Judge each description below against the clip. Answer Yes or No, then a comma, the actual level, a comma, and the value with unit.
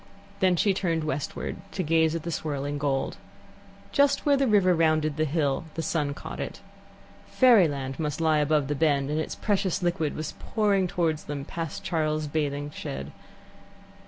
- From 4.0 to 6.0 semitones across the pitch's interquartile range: No, average, 3.3 semitones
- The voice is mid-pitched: Yes, medium, 155 Hz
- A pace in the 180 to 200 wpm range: No, average, 165 wpm